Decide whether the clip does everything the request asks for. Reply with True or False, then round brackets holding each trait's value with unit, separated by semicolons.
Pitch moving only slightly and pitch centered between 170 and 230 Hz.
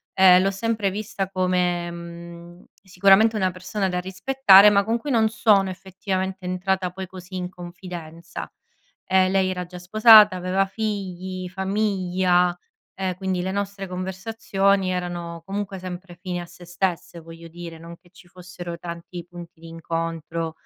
True (1.8 semitones; 185 Hz)